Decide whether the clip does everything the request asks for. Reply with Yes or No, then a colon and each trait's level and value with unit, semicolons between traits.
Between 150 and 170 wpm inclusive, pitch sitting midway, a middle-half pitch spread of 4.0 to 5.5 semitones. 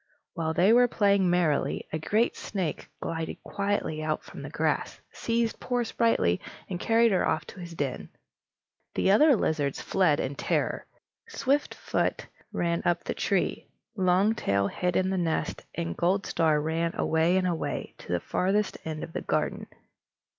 Yes: average, 155 wpm; medium, 180 Hz; average, 4.3 semitones